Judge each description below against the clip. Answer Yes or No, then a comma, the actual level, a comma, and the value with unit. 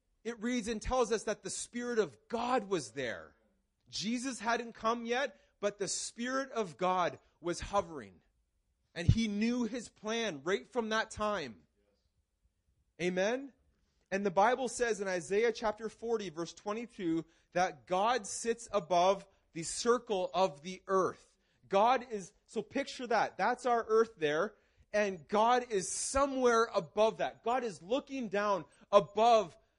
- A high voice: Yes, high, 215 Hz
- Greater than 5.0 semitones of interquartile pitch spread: No, average, 4.2 semitones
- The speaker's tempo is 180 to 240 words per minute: No, average, 145 wpm